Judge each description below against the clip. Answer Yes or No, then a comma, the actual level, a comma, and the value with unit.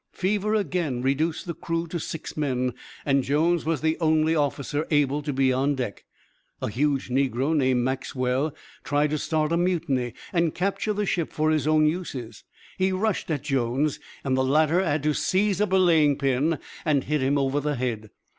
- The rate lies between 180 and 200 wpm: Yes, average, 185 wpm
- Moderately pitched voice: Yes, medium, 150 Hz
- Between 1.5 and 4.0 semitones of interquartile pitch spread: Yes, average, 3.6 semitones